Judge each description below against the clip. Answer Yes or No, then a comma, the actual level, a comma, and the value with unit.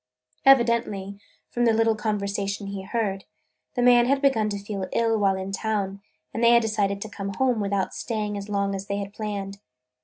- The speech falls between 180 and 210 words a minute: Yes, average, 190 wpm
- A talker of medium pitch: No, high, 210 Hz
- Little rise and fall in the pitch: Yes, narrow, 2.3 semitones